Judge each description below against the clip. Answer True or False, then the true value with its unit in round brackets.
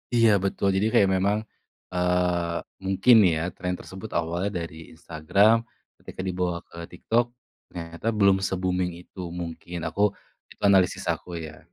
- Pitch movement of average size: False (2.3 semitones)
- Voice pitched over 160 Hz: False (90 Hz)